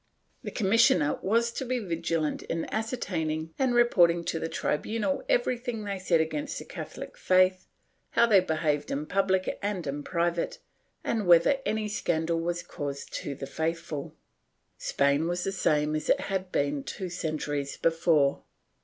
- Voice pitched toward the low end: No, medium, 170 Hz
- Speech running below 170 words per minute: Yes, average, 155 wpm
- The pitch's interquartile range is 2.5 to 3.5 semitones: No, average, 4.8 semitones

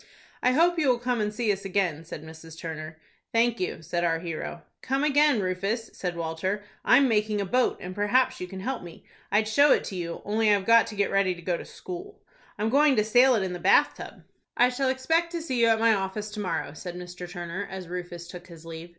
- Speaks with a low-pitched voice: No, high, 205 Hz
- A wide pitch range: Yes, wide, 5.7 semitones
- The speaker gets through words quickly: Yes, fast, 235 wpm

